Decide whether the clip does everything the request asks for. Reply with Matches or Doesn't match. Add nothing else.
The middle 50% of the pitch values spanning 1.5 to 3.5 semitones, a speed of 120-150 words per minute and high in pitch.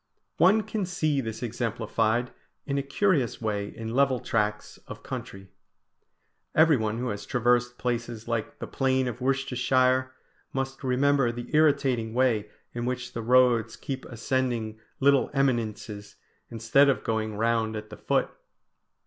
Doesn't match